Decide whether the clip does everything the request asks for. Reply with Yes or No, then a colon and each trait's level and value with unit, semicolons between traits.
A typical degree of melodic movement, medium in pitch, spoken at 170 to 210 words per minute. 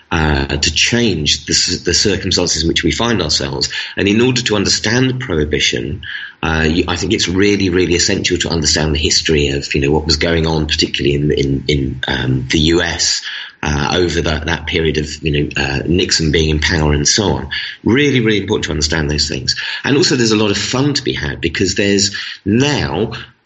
No: average, 4.5 semitones; very low, 85 Hz; average, 200 wpm